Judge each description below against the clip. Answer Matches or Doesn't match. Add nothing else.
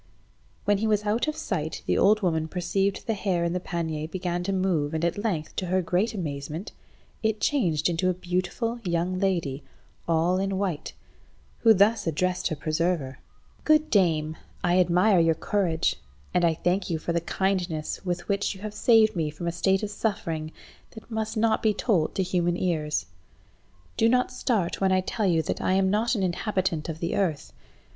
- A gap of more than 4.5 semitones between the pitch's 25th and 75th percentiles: Doesn't match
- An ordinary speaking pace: Matches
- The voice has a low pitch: Doesn't match